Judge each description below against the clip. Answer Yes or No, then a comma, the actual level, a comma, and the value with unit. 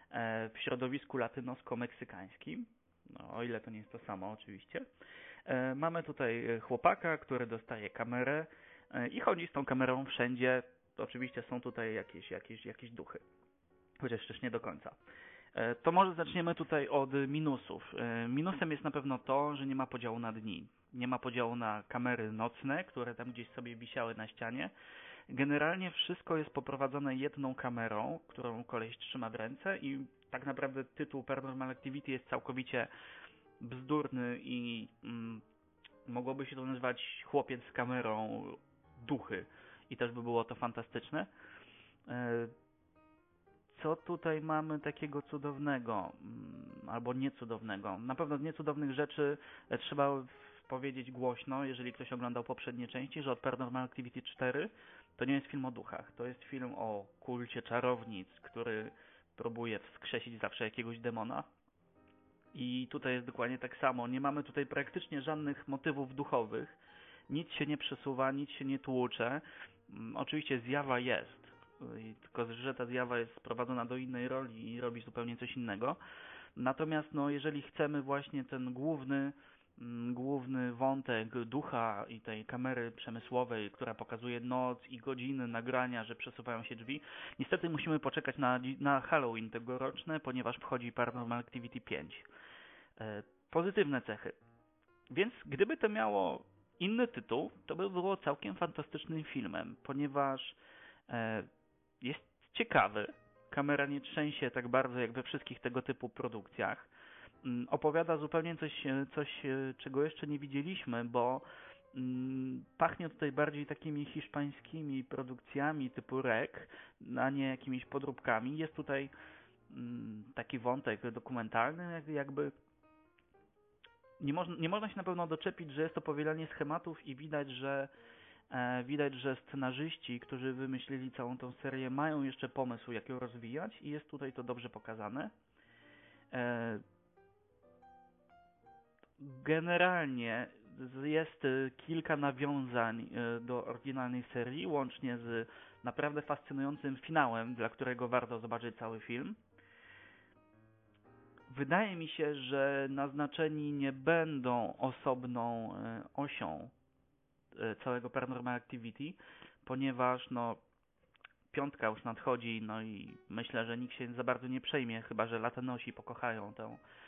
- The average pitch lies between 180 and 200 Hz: No, low, 130 Hz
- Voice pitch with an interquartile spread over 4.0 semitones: No, average, 3.3 semitones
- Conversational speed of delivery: Yes, average, 130 wpm